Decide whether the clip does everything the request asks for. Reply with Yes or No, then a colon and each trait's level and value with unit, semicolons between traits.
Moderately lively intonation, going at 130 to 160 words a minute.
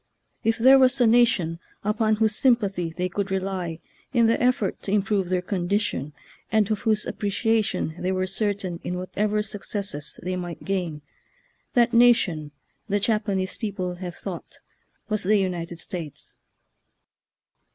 Yes: average, 3.4 semitones; average, 145 wpm